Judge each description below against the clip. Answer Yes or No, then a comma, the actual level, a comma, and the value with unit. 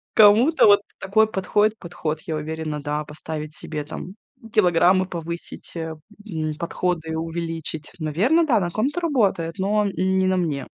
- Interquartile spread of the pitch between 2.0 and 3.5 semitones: No, average, 4.5 semitones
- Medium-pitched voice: Yes, medium, 170 Hz